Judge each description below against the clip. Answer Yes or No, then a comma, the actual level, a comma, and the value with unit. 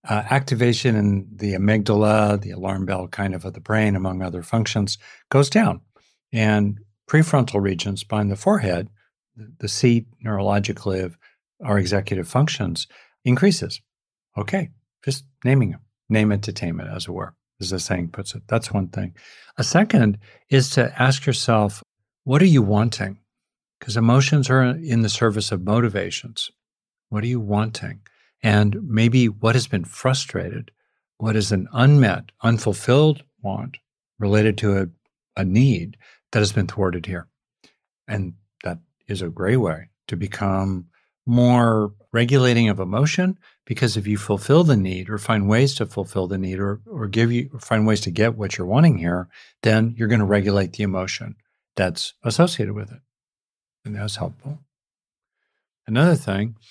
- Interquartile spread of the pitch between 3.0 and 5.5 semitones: Yes, average, 3.7 semitones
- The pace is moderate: Yes, average, 160 wpm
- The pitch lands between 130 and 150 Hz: No, low, 110 Hz